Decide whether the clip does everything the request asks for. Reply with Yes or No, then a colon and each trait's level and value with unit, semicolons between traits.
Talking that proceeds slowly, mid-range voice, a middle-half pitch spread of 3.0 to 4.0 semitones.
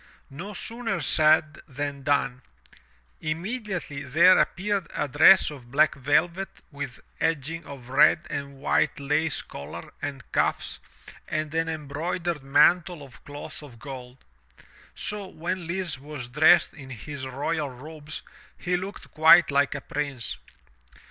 Yes: slow, 130 wpm; medium, 150 Hz; average, 3.4 semitones